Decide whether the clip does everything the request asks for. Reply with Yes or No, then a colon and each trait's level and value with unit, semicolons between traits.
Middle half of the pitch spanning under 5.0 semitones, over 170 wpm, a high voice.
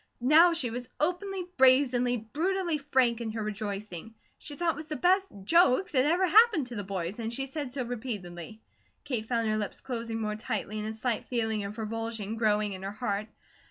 No: average, 5.3 semitones; average, 195 wpm; high, 235 Hz